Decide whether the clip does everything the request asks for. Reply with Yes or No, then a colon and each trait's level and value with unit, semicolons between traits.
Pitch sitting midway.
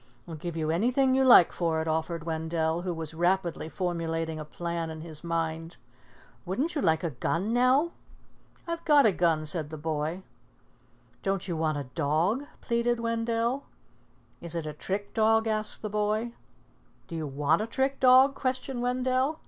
Yes: medium, 175 Hz